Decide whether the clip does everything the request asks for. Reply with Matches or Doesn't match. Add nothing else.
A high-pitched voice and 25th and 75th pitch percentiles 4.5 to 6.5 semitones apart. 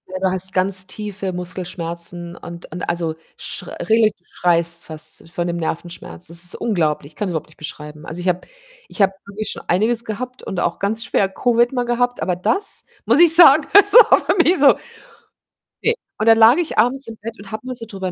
Matches